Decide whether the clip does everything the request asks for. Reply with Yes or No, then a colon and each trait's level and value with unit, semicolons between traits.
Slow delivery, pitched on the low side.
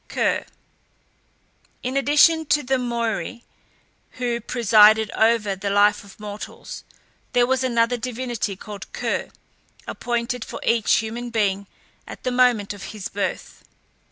No: slow, 130 wpm; high, 230 Hz